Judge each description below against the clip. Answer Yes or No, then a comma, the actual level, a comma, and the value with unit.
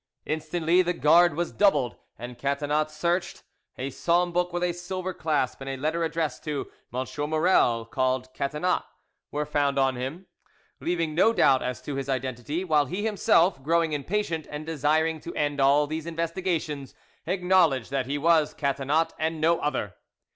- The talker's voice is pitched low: No, medium, 155 Hz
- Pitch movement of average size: Yes, average, 3.7 semitones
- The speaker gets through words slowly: No, average, 160 wpm